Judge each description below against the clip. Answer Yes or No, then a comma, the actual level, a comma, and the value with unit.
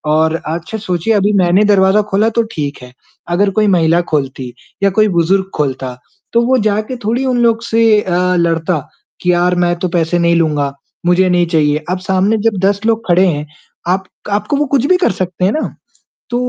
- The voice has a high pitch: No, medium, 180 Hz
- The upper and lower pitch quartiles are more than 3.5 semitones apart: Yes, average, 4.4 semitones